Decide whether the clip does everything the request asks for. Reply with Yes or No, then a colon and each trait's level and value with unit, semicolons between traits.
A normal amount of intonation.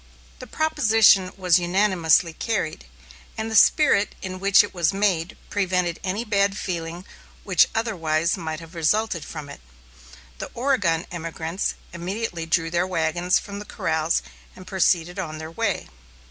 Yes: average, 3.6 semitones